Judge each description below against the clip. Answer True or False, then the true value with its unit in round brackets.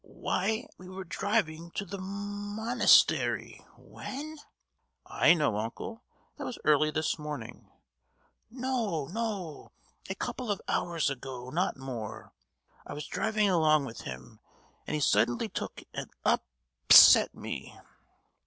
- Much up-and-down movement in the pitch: True (7.4 semitones)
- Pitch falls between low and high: True (170 Hz)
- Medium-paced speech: False (125 wpm)